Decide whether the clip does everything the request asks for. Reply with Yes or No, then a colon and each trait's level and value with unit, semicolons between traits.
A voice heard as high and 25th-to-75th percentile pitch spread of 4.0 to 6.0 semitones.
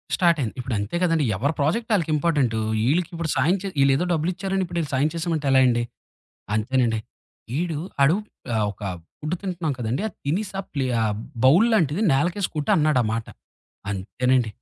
No: medium, 150 Hz; wide, 5.4 semitones